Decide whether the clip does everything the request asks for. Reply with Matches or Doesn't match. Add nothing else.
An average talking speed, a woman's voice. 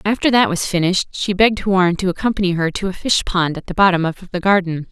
Doesn't match